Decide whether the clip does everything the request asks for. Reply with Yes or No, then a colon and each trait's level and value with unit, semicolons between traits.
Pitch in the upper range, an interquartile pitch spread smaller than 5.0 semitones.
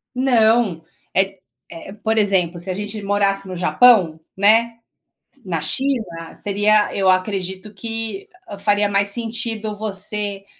Yes: high, 205 Hz; narrow, 2.5 semitones